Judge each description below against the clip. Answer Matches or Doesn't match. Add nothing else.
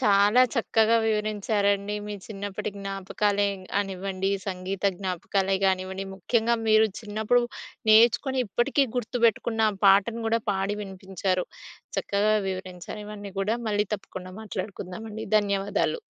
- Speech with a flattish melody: Matches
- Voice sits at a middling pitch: Doesn't match